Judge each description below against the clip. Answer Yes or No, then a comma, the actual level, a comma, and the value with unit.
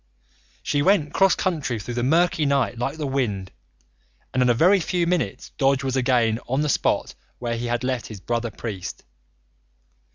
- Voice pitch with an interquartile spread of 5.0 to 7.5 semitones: No, average, 4.2 semitones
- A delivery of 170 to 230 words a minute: Yes, average, 175 wpm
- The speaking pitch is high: No, low, 130 Hz